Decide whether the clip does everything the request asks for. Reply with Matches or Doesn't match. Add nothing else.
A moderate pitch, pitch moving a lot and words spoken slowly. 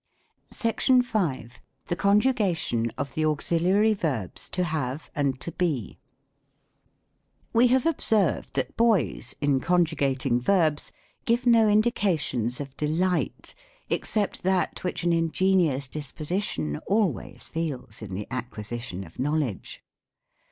Matches